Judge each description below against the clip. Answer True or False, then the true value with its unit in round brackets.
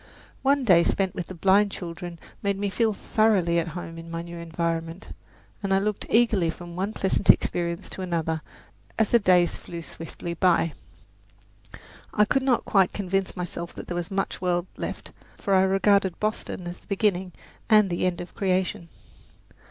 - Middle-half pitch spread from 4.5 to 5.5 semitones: False (2.7 semitones)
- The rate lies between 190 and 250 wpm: False (175 wpm)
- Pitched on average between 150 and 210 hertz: True (185 Hz)